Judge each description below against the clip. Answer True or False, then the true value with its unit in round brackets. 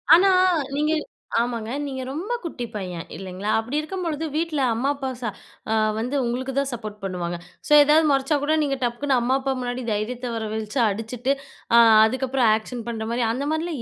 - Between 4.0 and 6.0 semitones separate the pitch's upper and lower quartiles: True (4.3 semitones)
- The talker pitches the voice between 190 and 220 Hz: False (250 Hz)